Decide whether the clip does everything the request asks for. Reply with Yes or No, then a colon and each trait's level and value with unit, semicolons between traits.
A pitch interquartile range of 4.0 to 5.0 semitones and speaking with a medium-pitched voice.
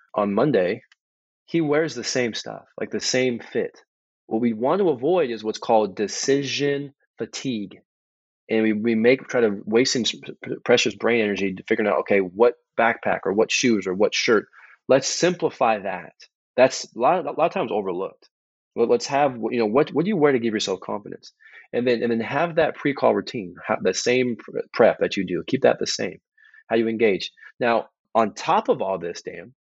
No: average, 4.7 semitones; low, 120 Hz